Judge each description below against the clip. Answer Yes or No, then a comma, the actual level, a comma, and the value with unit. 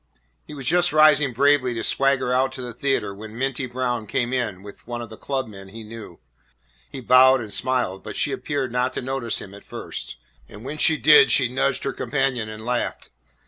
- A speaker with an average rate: No, fast, 210 wpm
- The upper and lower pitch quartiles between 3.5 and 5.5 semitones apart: No, average, 3.1 semitones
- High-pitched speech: No, low, 125 Hz